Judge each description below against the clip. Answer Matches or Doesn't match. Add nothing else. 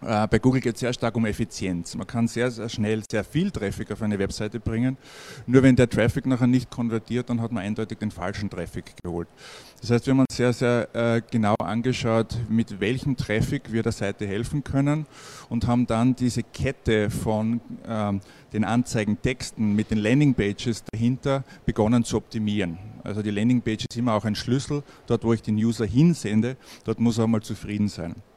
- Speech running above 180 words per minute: Matches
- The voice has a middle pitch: Doesn't match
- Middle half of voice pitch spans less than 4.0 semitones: Matches